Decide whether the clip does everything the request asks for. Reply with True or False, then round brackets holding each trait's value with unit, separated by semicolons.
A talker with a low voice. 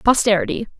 False (220 Hz)